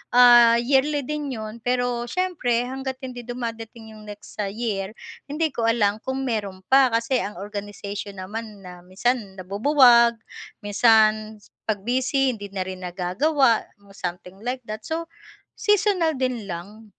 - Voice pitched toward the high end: Yes, high, 230 Hz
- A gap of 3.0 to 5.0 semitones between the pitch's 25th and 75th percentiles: Yes, average, 4.0 semitones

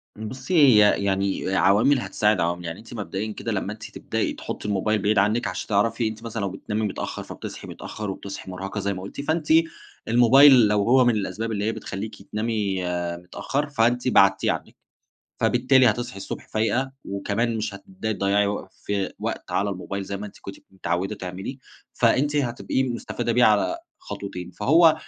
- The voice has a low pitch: Yes, low, 105 Hz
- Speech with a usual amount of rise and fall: Yes, average, 3.5 semitones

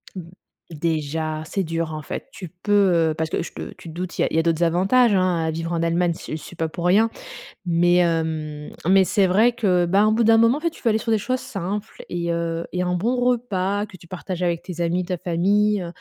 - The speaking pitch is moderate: Yes, medium, 180 Hz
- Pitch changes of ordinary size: Yes, average, 3.6 semitones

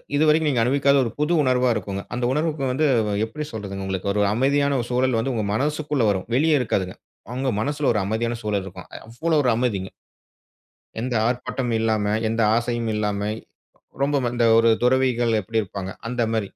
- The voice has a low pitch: Yes, low, 120 Hz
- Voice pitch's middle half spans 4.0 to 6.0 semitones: Yes, average, 4.4 semitones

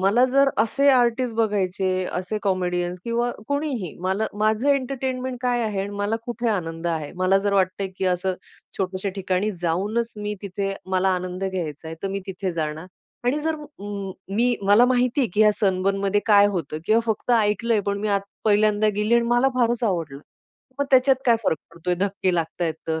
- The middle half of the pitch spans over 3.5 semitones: Yes, average, 4.1 semitones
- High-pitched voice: Yes, high, 205 Hz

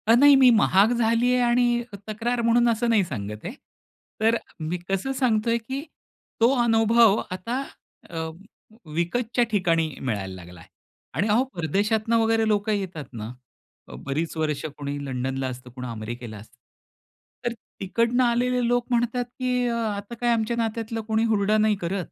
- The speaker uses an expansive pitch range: Yes, wide, 6.5 semitones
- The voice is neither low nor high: No, high, 220 Hz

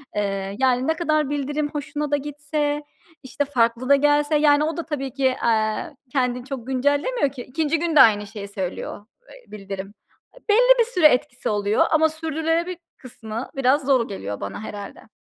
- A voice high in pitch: Yes, very high, 275 Hz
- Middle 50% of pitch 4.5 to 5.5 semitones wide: Yes, average, 4.8 semitones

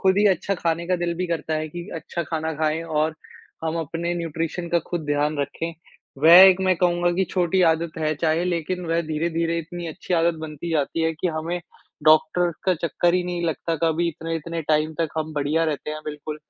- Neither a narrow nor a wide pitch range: No, narrow, 1.8 semitones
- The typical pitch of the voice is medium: Yes, medium, 165 Hz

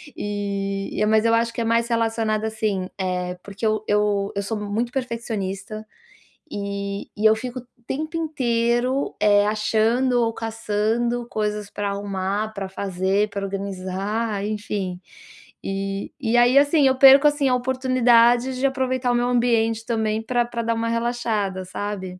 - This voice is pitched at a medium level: No, high, 220 Hz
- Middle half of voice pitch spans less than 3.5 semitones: Yes, average, 3.1 semitones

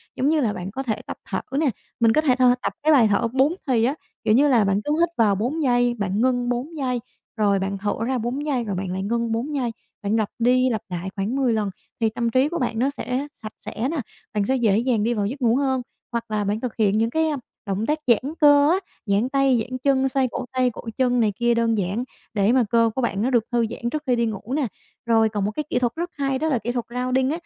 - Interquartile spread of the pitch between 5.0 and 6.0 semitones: No, average, 3.4 semitones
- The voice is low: No, high, 240 Hz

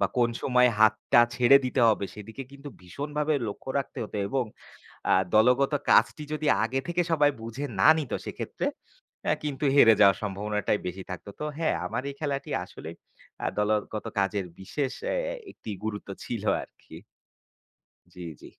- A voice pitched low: Yes, low, 120 Hz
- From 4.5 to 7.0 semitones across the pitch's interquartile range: Yes, average, 5.0 semitones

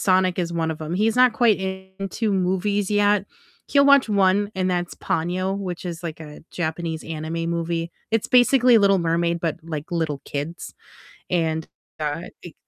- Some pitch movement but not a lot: Yes, average, 3.4 semitones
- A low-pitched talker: No, medium, 180 Hz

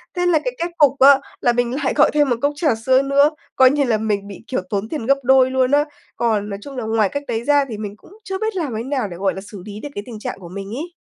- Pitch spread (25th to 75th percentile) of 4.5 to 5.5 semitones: Yes, average, 5.1 semitones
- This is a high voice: Yes, very high, 255 Hz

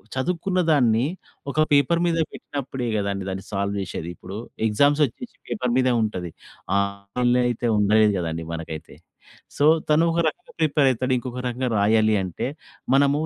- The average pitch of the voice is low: Yes, low, 120 Hz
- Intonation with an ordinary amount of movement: No, wide, 6.1 semitones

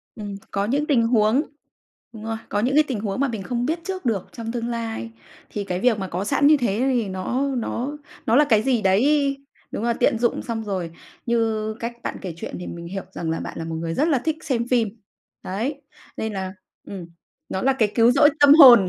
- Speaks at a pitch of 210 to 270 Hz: Yes, high, 230 Hz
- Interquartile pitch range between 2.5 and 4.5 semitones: No, average, 4.9 semitones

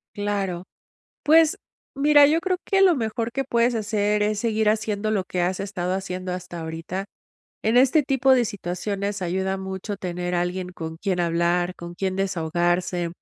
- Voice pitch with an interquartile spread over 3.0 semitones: Yes, average, 3.9 semitones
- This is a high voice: Yes, high, 195 Hz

